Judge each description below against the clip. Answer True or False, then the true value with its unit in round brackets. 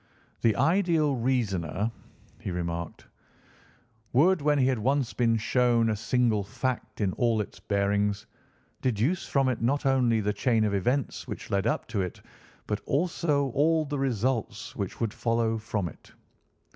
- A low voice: True (115 Hz)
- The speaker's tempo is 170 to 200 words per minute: False (160 wpm)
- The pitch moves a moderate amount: True (4.7 semitones)